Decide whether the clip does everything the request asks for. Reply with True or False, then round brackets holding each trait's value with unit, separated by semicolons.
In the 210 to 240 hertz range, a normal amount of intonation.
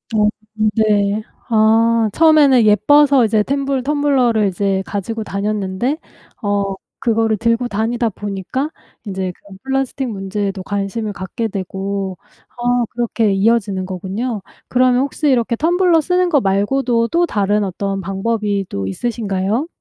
True (220 Hz; 4.2 semitones)